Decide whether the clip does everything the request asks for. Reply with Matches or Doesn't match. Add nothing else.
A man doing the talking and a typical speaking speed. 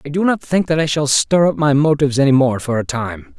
Doesn't match